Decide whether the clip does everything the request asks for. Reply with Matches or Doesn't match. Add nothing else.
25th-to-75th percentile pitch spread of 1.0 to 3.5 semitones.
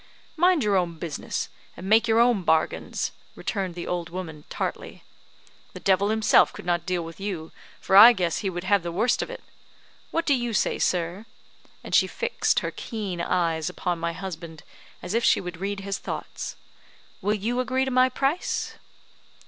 Doesn't match